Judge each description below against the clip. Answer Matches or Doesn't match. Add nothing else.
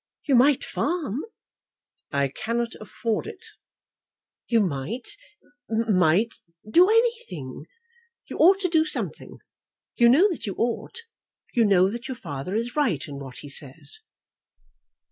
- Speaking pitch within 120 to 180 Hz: Doesn't match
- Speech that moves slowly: Matches